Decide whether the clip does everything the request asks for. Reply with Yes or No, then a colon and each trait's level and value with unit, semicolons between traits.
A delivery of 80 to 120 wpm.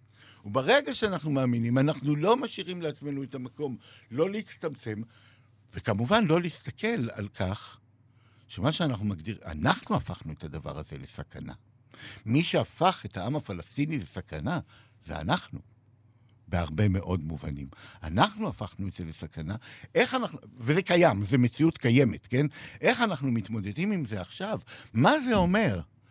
No: average, 135 wpm